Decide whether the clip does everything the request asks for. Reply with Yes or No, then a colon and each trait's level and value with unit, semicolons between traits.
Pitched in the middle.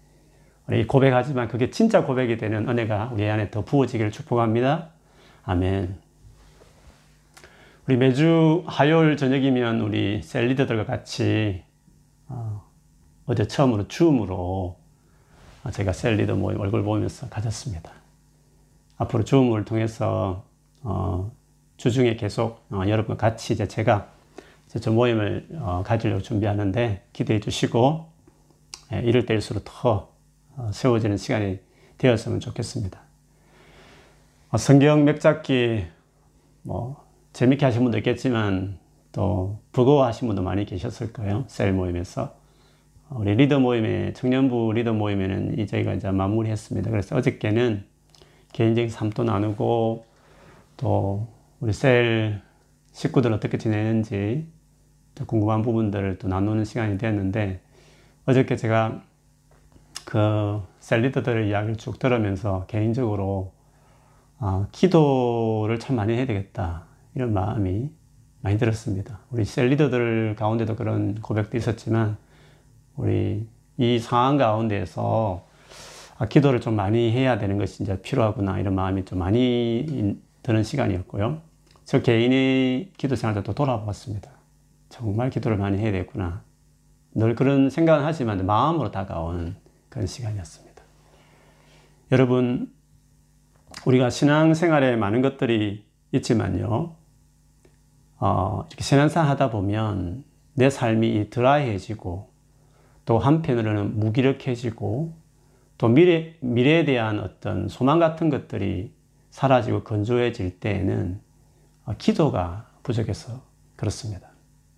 No: low, 115 Hz